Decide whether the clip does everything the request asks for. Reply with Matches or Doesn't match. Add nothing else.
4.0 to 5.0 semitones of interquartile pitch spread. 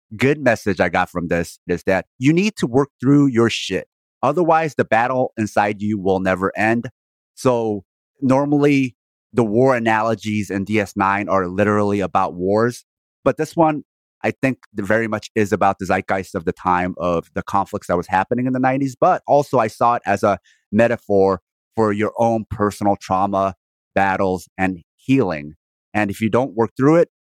Matches